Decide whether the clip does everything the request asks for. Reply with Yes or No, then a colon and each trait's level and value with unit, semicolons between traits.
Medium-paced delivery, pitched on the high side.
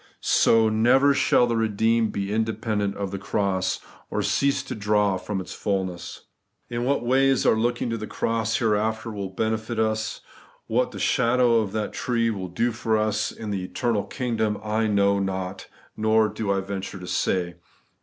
No: average, 175 wpm; low, 110 Hz